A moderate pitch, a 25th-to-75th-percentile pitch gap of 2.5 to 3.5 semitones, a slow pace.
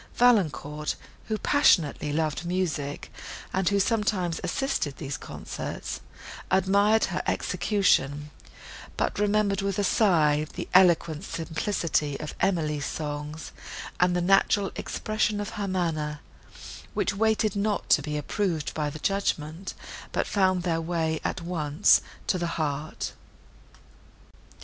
No: medium, 175 Hz; average, 4.7 semitones; slow, 125 wpm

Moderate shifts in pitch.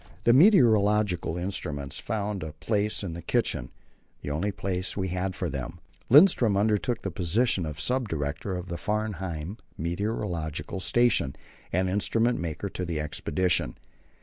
Yes: average, 4.3 semitones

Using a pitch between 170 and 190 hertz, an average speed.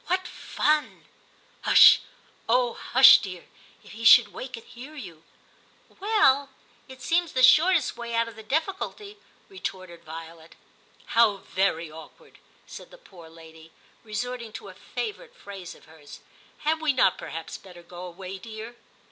No: high, 230 Hz; average, 170 wpm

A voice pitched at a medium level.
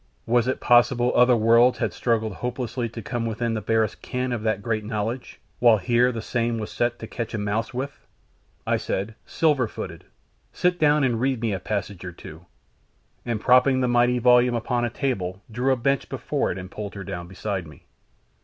No: low, 115 Hz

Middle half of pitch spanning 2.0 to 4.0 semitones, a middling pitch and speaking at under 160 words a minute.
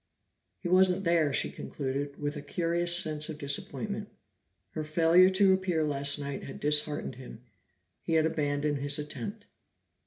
Yes: average, 3.5 semitones; medium, 155 Hz; average, 150 wpm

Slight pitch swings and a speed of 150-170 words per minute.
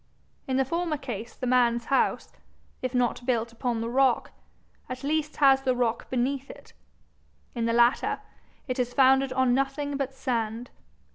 Yes: narrow, 2.2 semitones; average, 160 wpm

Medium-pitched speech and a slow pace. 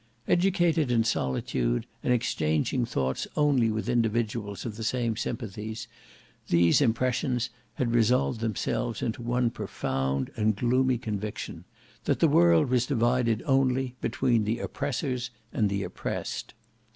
No: low, 115 Hz; slow, 125 wpm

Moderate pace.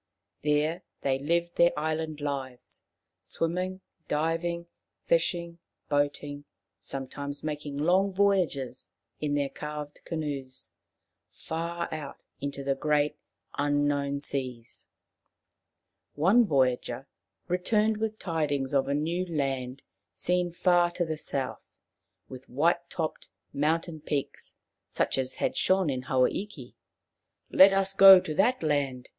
No: slow, 120 wpm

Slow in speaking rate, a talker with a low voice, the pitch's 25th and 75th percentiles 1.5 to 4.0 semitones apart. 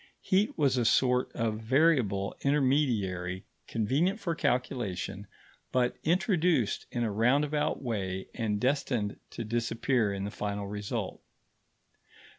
No: slow, 115 wpm; low, 120 Hz; wide, 5.5 semitones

